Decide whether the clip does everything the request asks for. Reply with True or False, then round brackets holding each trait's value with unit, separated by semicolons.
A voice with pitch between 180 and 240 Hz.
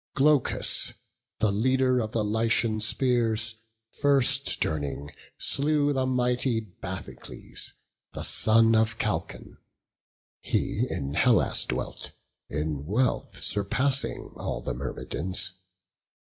False (115 Hz)